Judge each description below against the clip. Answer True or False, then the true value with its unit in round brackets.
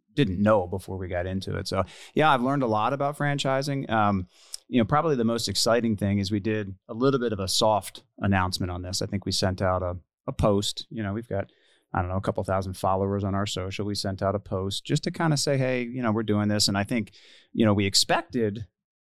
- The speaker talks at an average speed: False (250 wpm)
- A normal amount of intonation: True (3.3 semitones)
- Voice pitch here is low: True (105 Hz)